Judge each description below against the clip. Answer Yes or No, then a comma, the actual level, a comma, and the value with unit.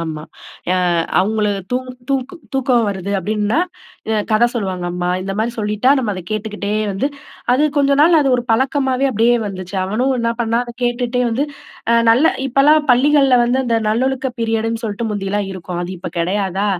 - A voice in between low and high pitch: No, high, 225 Hz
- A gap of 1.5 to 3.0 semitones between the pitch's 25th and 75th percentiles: No, average, 4.1 semitones